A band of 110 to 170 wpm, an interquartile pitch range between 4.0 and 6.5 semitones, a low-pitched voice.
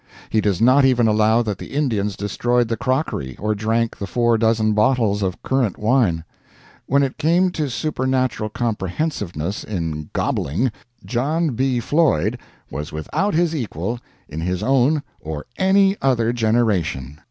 Yes: average, 145 wpm; average, 5.0 semitones; low, 115 Hz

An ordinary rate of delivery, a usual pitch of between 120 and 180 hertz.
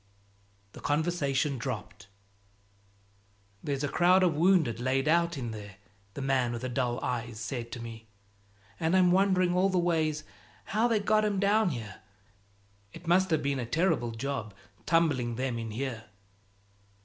Yes: average, 150 wpm; medium, 140 Hz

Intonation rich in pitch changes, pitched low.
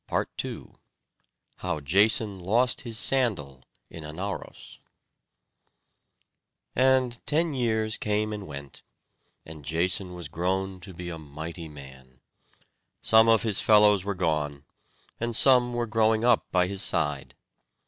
Yes: wide, 5.9 semitones; very low, 95 Hz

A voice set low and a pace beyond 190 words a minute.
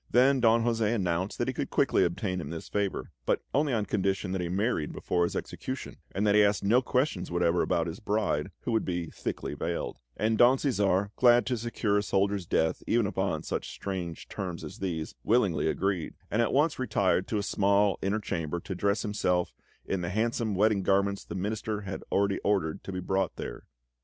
Yes: low, 100 Hz; average, 200 wpm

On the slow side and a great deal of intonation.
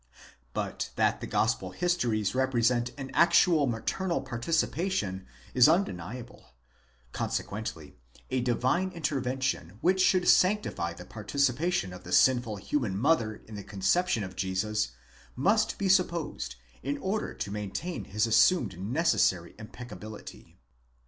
Yes: slow, 120 wpm; wide, 8.5 semitones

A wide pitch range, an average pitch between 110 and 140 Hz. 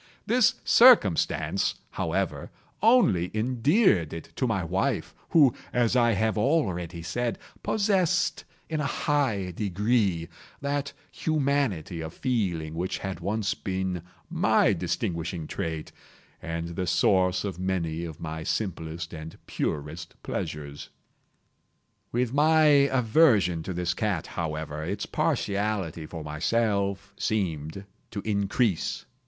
No: wide, 6.7 semitones; very low, 95 Hz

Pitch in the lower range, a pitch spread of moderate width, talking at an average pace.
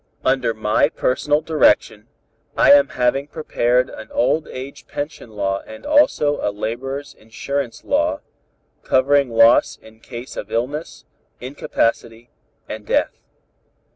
No: low, 125 Hz; average, 4.2 semitones; slow, 120 wpm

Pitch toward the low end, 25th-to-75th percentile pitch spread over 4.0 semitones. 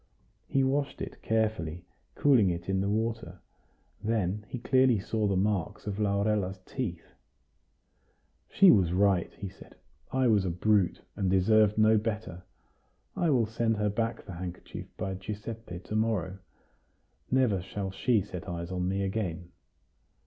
No: low, 100 Hz; average, 3.3 semitones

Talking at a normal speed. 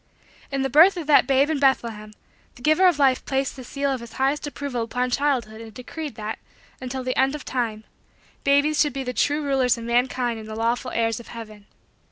No: fast, 215 wpm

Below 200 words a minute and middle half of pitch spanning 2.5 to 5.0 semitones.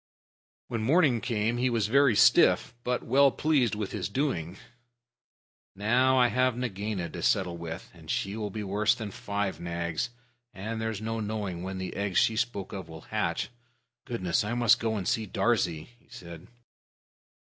Yes: average, 170 wpm; average, 4.1 semitones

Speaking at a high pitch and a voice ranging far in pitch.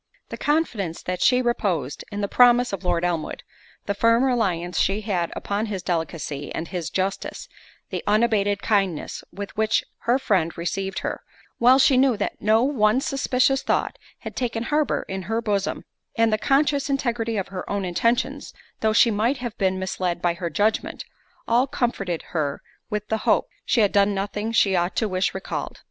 No: high, 205 Hz; average, 4.3 semitones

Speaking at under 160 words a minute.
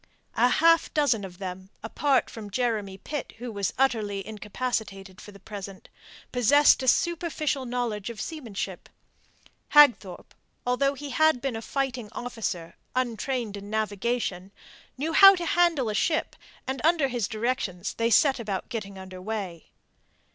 Yes: average, 145 wpm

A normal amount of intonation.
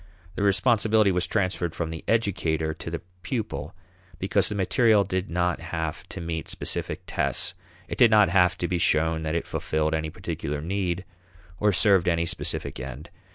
Yes: average, 3.6 semitones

